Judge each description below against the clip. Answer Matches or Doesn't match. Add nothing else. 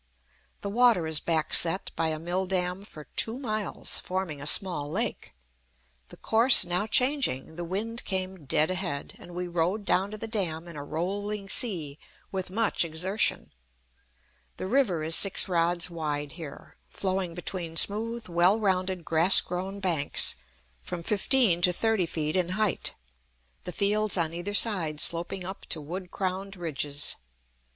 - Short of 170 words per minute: Matches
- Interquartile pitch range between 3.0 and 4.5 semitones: Matches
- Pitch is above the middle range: Doesn't match